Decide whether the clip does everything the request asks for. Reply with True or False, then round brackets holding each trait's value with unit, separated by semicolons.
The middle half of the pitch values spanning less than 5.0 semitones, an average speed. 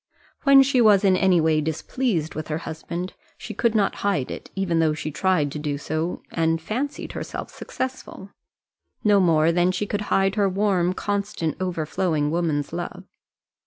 True (4.1 semitones; 165 wpm)